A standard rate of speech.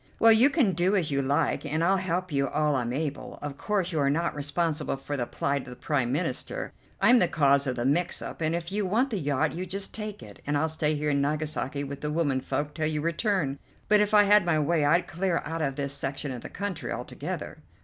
No: fast, 240 wpm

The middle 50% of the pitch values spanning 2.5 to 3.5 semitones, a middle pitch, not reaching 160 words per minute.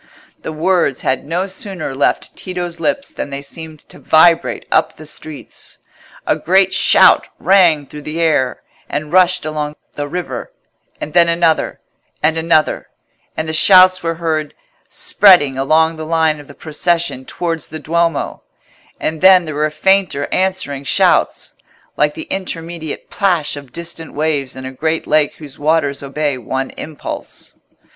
Yes: average, 2.8 semitones; medium, 160 Hz; average, 150 wpm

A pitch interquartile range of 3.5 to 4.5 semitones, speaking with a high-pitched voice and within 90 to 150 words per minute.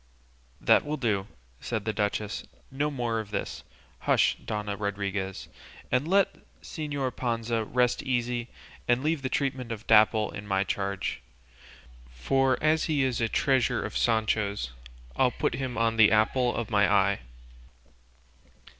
No: average, 4.0 semitones; low, 115 Hz; average, 145 wpm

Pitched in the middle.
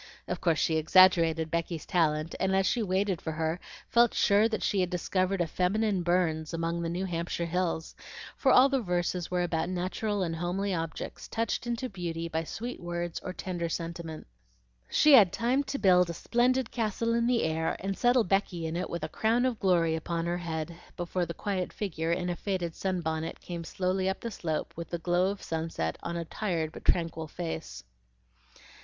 Yes: medium, 175 Hz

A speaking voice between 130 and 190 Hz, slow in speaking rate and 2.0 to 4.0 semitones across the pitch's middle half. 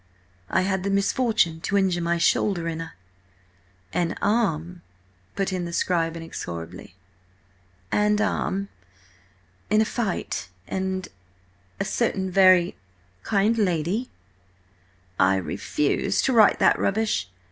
Yes: medium, 185 Hz; slow, 115 wpm; average, 3.6 semitones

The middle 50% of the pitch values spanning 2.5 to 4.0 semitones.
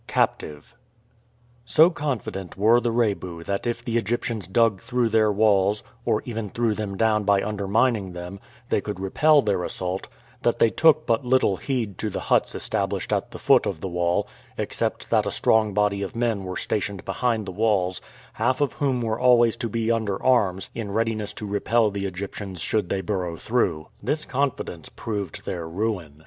Yes: average, 3.5 semitones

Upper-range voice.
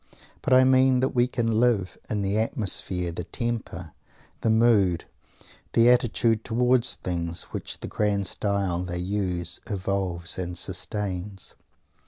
No: low, 105 Hz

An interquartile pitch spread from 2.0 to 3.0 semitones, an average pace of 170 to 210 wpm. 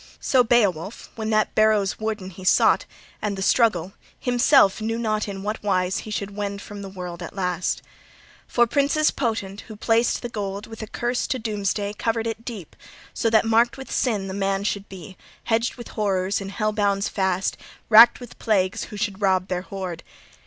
Yes: average, 2.7 semitones; average, 190 wpm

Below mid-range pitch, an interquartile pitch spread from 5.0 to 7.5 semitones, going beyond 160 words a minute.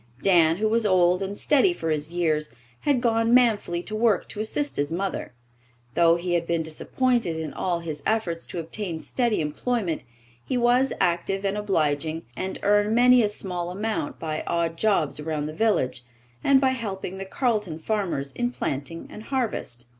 No: high, 190 Hz; wide, 5.4 semitones; average, 175 wpm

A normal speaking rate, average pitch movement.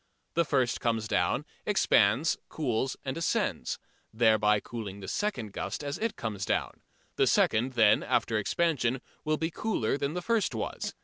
No: average, 160 wpm; wide, 6.3 semitones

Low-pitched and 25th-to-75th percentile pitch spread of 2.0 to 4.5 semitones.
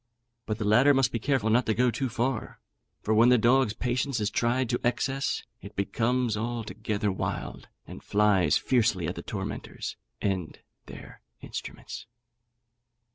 Yes: low, 115 Hz; average, 3.1 semitones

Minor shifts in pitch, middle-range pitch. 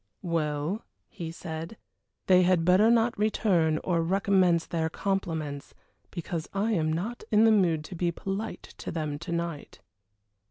No: average, 3.5 semitones; medium, 175 Hz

